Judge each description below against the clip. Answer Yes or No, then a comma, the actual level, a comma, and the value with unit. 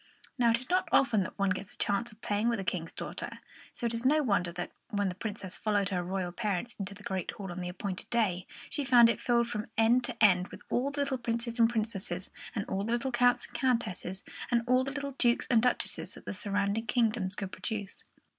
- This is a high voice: Yes, high, 220 Hz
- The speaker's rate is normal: No, fast, 235 wpm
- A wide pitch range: No, average, 3.6 semitones